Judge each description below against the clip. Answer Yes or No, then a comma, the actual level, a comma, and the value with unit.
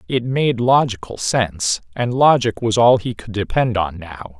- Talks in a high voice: No, low, 110 Hz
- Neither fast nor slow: Yes, average, 165 wpm